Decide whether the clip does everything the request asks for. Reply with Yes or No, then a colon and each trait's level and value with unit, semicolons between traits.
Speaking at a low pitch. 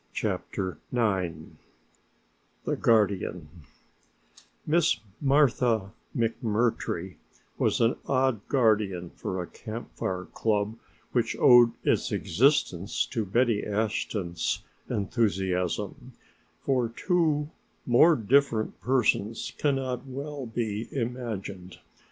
Yes: low, 115 Hz